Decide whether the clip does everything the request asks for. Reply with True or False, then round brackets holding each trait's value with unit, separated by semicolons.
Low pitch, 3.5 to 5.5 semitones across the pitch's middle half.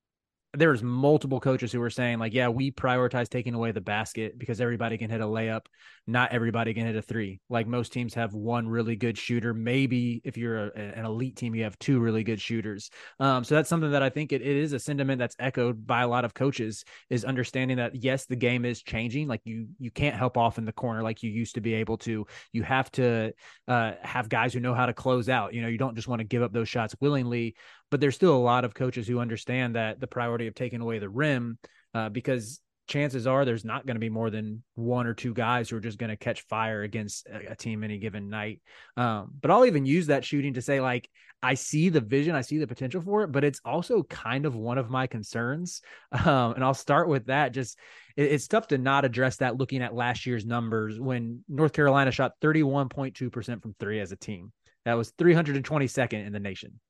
False (120 Hz; 2.8 semitones)